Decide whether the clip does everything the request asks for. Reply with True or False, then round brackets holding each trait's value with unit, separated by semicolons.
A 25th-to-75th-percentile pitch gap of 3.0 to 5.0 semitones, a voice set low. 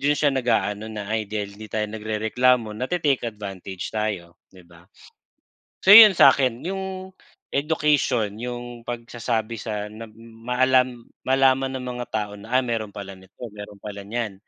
True (3.7 semitones; 115 Hz)